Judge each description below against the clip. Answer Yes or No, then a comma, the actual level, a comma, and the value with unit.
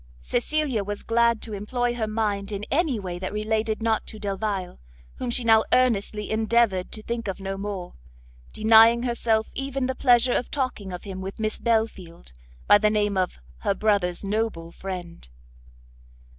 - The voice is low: No, high, 215 Hz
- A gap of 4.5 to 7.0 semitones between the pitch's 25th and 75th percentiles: No, average, 3.0 semitones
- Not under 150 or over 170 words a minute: Yes, average, 165 wpm